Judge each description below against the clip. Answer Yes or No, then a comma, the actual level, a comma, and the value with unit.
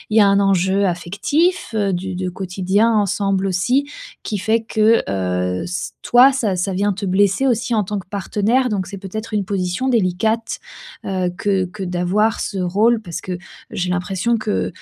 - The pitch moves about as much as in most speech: Yes, average, 3.2 semitones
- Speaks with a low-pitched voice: No, high, 195 Hz